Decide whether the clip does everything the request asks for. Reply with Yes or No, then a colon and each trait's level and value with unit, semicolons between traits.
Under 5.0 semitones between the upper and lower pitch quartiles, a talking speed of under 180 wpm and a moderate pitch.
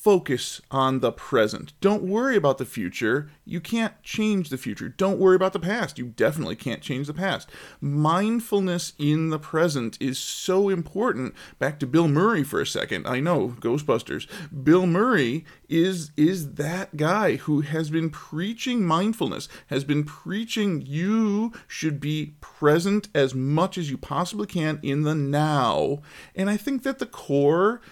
No: average, 5.3 semitones; average, 160 wpm; medium, 165 Hz